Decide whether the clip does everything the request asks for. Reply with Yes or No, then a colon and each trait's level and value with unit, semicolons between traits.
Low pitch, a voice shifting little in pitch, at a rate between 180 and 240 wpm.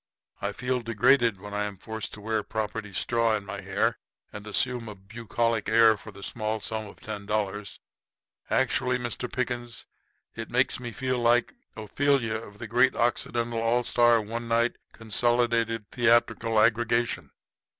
No: low, 115 Hz; narrow, 2.0 semitones; average, 160 wpm